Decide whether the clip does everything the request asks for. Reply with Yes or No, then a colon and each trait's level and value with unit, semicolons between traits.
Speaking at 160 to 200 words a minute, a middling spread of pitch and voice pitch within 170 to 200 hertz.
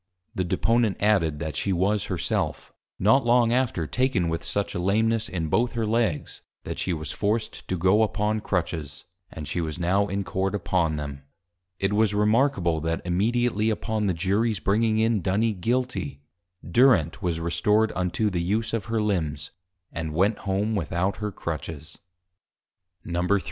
No: average, 165 wpm; average, 4.4 semitones; low, 100 Hz